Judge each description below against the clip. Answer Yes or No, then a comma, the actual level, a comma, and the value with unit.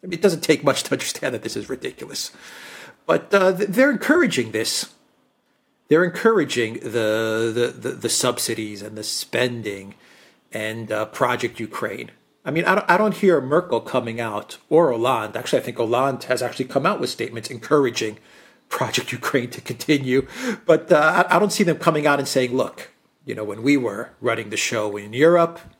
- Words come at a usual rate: Yes, average, 185 wpm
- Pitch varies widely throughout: Yes, wide, 8.0 semitones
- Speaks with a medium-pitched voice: Yes, medium, 145 Hz